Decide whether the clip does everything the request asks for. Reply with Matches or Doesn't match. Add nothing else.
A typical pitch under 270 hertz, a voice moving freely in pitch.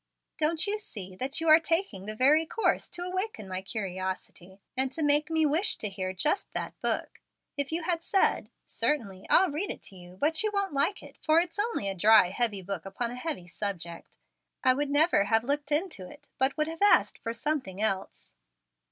Doesn't match